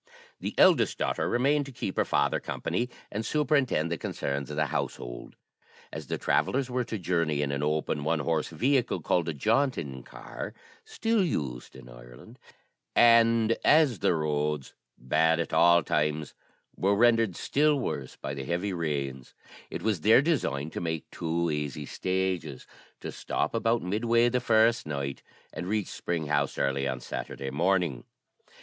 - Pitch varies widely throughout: Yes, wide, 7.9 semitones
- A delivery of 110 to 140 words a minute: No, average, 160 wpm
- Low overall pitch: Yes, very low, 85 Hz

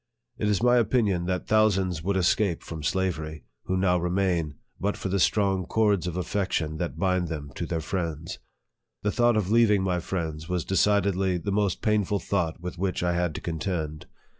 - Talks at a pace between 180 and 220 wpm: Yes, average, 185 wpm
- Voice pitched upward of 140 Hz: No, very low, 90 Hz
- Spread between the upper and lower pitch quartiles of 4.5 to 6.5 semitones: No, average, 3.0 semitones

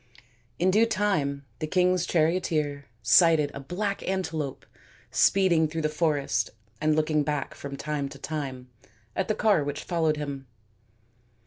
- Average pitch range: Yes, average, 4.1 semitones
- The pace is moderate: Yes, average, 145 wpm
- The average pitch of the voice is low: No, medium, 155 Hz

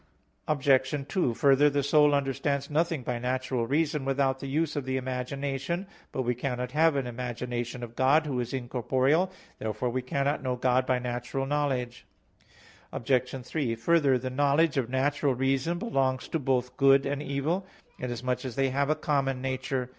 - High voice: No, low, 135 Hz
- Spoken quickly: No, average, 170 wpm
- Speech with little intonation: Yes, narrow, 2.2 semitones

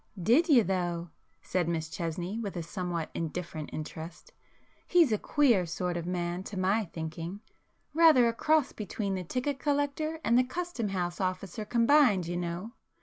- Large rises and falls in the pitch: Yes, wide, 6.3 semitones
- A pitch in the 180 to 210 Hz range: Yes, high, 190 Hz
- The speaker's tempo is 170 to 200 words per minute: No, average, 150 wpm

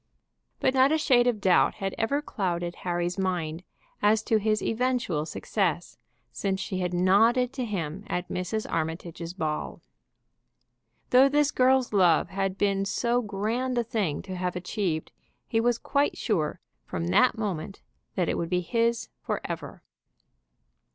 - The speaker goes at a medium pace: Yes, average, 150 wpm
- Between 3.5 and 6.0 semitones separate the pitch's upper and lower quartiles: Yes, average, 5.0 semitones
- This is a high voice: Yes, high, 195 Hz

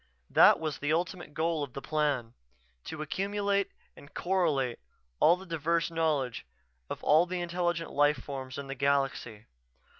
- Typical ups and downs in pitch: Yes, average, 3.8 semitones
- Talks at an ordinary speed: Yes, average, 150 wpm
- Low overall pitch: No, medium, 155 Hz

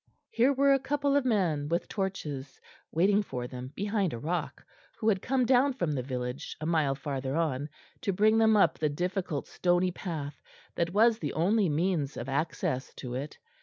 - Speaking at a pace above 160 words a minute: Yes, average, 185 wpm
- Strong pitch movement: Yes, wide, 6.8 semitones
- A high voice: No, medium, 170 Hz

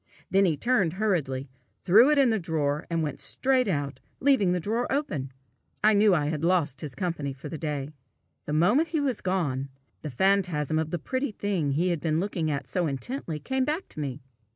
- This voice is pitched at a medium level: Yes, medium, 170 Hz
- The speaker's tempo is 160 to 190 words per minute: No, average, 200 wpm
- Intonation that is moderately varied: No, wide, 6.2 semitones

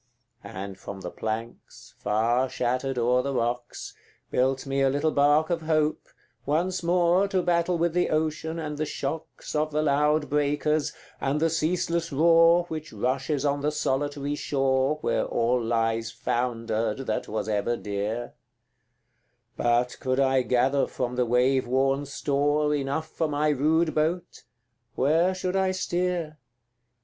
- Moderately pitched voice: Yes, medium, 145 Hz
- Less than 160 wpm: Yes, average, 145 wpm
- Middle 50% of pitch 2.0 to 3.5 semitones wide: No, average, 4.2 semitones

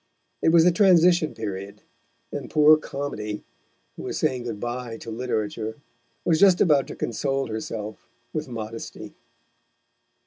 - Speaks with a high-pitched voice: No, low, 125 Hz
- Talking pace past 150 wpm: No, slow, 135 wpm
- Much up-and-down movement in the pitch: Yes, wide, 6.0 semitones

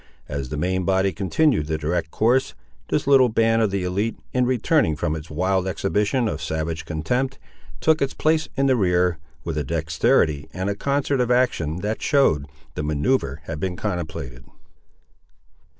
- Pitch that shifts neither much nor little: No, wide, 7.7 semitones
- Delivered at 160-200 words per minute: Yes, average, 165 wpm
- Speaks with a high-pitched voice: No, very low, 95 Hz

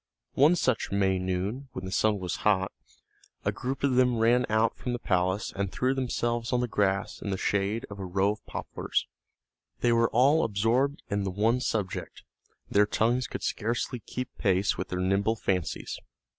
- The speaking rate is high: No, average, 185 wpm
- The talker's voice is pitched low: Yes, low, 110 Hz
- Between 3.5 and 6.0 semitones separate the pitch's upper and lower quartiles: Yes, average, 4.1 semitones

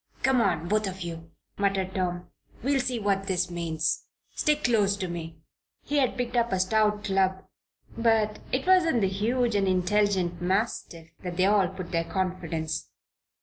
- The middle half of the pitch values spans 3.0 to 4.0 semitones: Yes, average, 3.7 semitones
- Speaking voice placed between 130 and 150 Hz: No, high, 195 Hz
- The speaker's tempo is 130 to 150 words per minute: No, average, 170 wpm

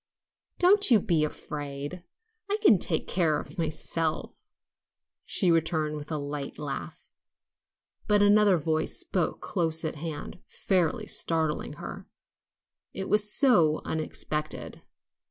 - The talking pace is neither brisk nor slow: No, slow, 120 wpm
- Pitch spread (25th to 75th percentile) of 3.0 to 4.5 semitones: Yes, average, 4.0 semitones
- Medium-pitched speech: Yes, medium, 160 Hz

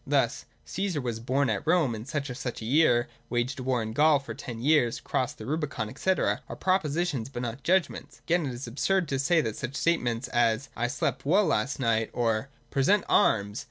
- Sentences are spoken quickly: Yes, fast, 215 wpm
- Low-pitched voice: Yes, low, 130 Hz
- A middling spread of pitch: Yes, average, 4.8 semitones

